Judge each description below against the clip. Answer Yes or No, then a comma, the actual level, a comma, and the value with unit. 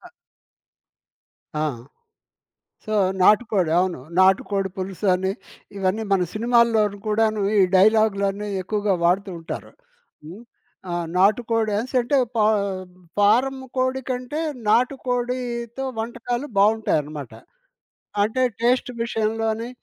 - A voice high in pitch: Yes, high, 220 Hz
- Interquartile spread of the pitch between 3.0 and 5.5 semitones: Yes, average, 3.6 semitones